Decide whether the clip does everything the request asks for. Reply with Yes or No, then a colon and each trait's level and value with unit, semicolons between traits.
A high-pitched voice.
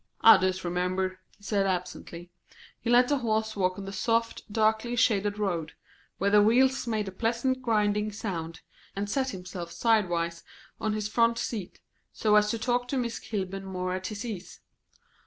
Yes: high, 210 Hz